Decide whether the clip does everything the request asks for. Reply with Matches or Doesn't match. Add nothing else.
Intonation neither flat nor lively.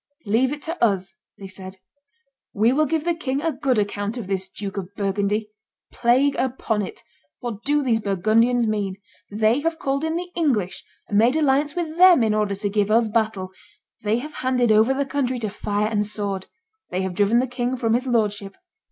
Matches